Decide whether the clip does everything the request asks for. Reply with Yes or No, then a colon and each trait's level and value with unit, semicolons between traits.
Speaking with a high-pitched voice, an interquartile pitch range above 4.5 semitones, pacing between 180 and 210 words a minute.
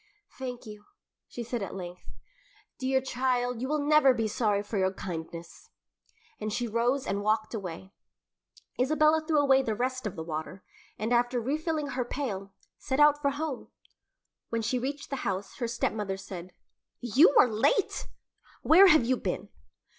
No: high, 240 Hz; average, 4.9 semitones; average, 160 wpm